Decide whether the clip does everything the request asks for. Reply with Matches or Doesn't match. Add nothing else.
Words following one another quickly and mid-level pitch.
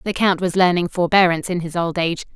Matches